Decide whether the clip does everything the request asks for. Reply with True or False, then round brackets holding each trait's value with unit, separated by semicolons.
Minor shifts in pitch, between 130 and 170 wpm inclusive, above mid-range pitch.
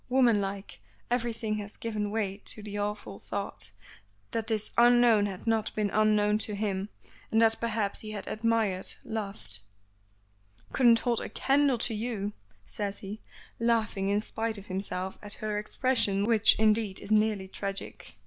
True (2.0 semitones; 150 wpm; 215 Hz)